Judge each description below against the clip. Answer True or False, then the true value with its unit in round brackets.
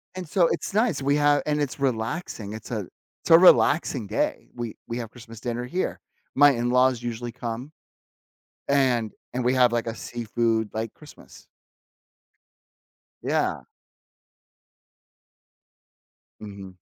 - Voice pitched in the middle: False (120 Hz)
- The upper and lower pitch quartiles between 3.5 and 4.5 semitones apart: True (4.0 semitones)